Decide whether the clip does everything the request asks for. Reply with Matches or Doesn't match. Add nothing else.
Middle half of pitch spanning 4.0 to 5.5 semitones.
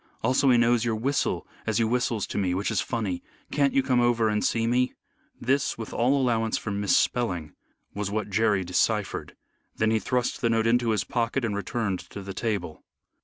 Doesn't match